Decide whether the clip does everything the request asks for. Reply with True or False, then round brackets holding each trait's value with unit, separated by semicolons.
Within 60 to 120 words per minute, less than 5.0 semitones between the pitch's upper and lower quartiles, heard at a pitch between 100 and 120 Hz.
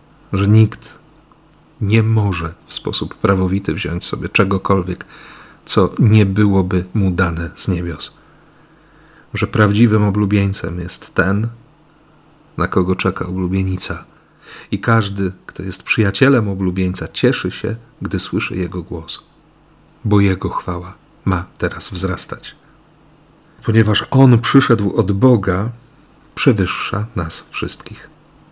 False (110 wpm; 5.5 semitones; 105 Hz)